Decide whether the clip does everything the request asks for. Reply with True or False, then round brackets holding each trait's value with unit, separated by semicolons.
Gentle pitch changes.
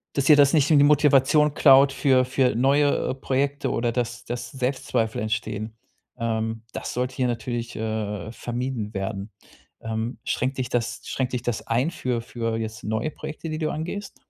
False (3.6 semitones)